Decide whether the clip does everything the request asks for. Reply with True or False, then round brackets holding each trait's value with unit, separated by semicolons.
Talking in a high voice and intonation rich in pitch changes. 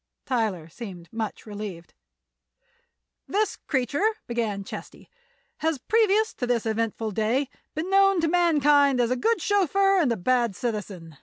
True (245 Hz; 8.2 semitones)